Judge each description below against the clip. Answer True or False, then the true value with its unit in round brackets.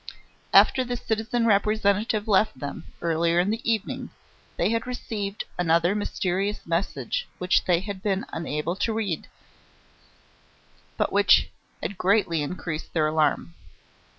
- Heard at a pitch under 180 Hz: False (195 Hz)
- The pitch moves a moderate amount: True (4.4 semitones)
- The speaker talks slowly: True (125 wpm)